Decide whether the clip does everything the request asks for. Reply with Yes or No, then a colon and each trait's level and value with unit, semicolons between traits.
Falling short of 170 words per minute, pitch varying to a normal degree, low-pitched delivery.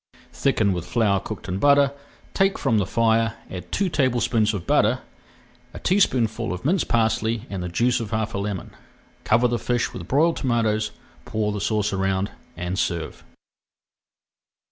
Yes: average, 160 wpm; average, 3.6 semitones; low, 110 Hz